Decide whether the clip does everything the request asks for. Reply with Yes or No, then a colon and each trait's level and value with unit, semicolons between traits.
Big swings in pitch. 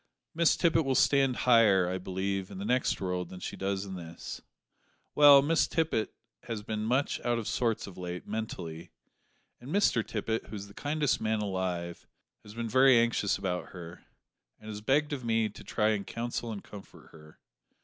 No: average, 4.7 semitones